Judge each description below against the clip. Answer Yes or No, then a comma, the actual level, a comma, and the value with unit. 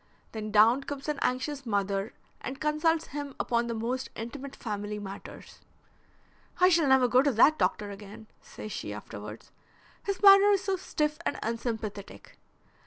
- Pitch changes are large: Yes, wide, 6.0 semitones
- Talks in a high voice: Yes, very high, 250 Hz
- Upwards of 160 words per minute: No, average, 155 wpm